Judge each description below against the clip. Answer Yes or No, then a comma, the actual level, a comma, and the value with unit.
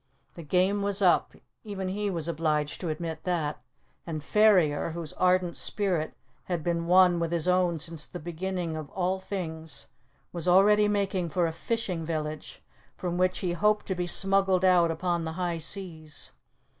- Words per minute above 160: Yes, average, 170 wpm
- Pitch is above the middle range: No, medium, 175 Hz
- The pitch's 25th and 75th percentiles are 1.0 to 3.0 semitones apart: Yes, narrow, 2.5 semitones